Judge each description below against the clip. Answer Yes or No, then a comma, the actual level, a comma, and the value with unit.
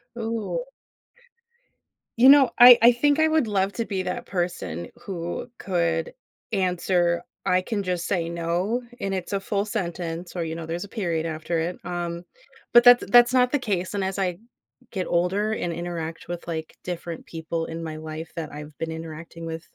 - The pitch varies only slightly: No, average, 3.6 semitones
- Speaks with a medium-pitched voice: Yes, medium, 175 Hz